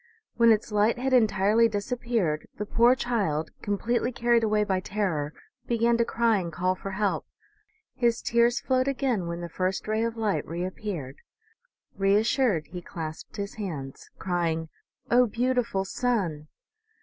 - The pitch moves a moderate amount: Yes, average, 4.5 semitones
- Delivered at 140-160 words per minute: Yes, average, 150 wpm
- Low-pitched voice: No, high, 210 Hz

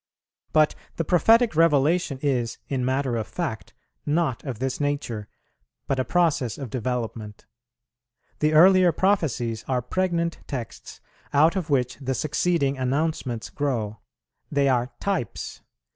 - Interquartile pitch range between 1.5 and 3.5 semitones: No, average, 4.9 semitones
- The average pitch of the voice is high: No, medium, 140 Hz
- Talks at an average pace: No, slow, 130 wpm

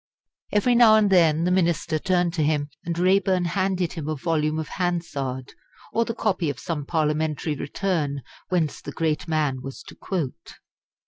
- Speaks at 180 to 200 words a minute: No, average, 170 wpm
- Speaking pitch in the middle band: Yes, medium, 165 Hz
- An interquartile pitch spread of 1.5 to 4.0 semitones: Yes, average, 3.5 semitones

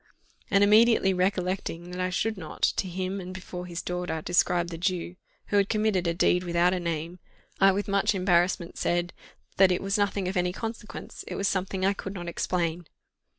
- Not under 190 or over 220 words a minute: Yes, average, 195 wpm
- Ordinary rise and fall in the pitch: No, narrow, 2.0 semitones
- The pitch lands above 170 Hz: Yes, medium, 185 Hz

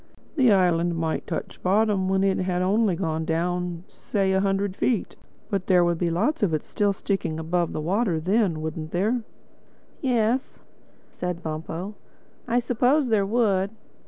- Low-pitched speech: No, high, 190 Hz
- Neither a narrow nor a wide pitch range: Yes, average, 3.8 semitones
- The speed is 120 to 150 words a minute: No, average, 160 wpm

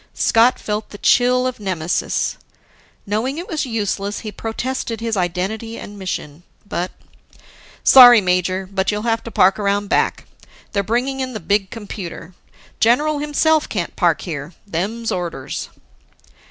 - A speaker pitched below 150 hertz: No, high, 210 Hz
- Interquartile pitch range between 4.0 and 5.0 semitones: Yes, average, 4.4 semitones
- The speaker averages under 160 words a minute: Yes, average, 140 wpm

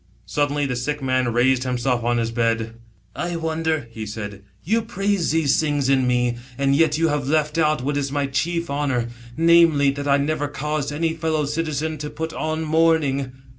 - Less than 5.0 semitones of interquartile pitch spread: Yes, average, 3.7 semitones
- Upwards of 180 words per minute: Yes, average, 195 wpm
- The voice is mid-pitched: Yes, medium, 145 Hz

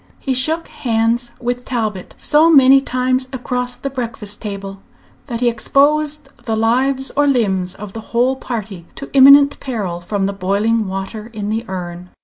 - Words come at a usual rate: Yes, average, 160 wpm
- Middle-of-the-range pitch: No, high, 235 Hz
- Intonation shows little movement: No, average, 4.5 semitones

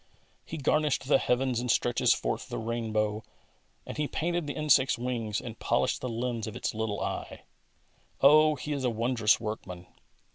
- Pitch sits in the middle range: No, low, 125 Hz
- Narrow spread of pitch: No, average, 4.2 semitones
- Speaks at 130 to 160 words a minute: No, average, 175 wpm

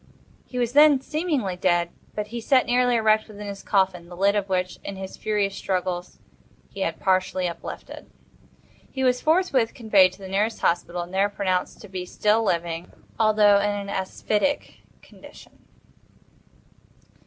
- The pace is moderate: Yes, average, 155 wpm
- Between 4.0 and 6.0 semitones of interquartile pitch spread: No, average, 3.5 semitones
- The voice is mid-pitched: No, high, 200 Hz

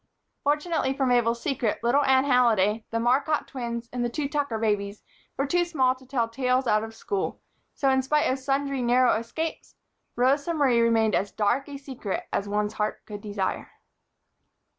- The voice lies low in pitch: No, very high, 250 Hz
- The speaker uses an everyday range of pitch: Yes, average, 3.6 semitones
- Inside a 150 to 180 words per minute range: Yes, average, 175 wpm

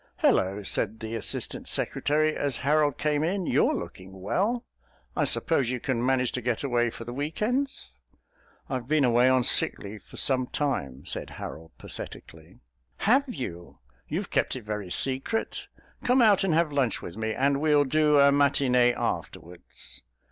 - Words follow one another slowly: No, average, 160 wpm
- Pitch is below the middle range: Yes, low, 130 Hz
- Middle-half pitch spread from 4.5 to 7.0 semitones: Yes, average, 4.9 semitones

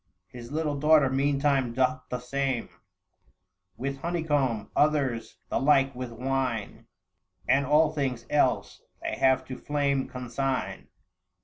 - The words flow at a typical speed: No, slow, 120 wpm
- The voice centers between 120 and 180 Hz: Yes, low, 135 Hz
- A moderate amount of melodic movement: No, narrow, 2.3 semitones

